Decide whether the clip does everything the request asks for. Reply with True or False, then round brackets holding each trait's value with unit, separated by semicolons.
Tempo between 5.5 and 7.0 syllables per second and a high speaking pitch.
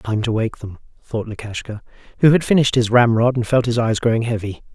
False (6.0 syllables/s; 115 Hz)